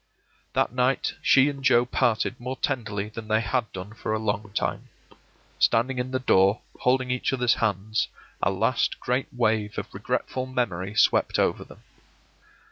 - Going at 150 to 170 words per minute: Yes, average, 160 wpm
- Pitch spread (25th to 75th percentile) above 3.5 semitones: No, average, 3.0 semitones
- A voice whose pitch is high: No, low, 115 Hz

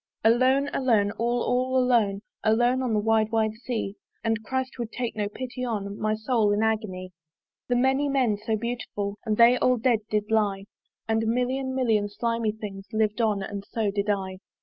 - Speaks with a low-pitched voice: No, high, 220 Hz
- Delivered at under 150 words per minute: No, average, 185 wpm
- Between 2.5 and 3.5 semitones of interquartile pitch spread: Yes, average, 3.0 semitones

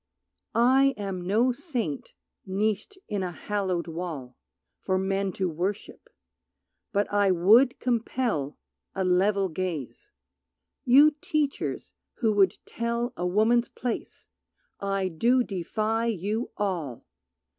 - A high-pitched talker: Yes, high, 205 Hz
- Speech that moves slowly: Yes, slow, 115 wpm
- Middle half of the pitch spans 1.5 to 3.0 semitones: No, average, 4.3 semitones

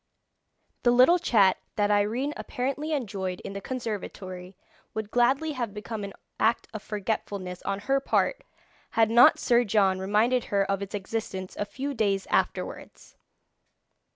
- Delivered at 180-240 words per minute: No, average, 145 wpm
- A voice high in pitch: Yes, high, 215 Hz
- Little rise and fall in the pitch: No, average, 3.8 semitones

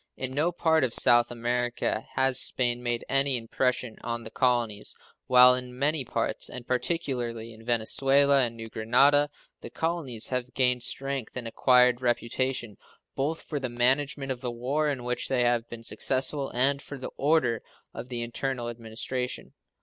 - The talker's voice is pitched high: No, low, 125 Hz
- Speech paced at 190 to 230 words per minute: No, average, 165 wpm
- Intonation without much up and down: Yes, narrow, 2.3 semitones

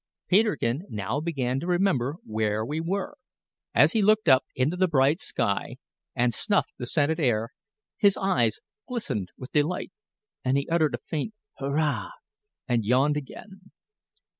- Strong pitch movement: Yes, wide, 6.7 semitones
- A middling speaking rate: Yes, average, 145 wpm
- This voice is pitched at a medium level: Yes, medium, 145 Hz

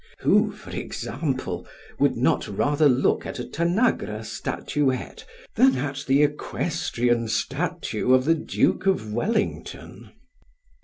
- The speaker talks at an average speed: No, slow, 115 wpm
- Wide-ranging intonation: No, average, 4.6 semitones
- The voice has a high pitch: No, low, 135 Hz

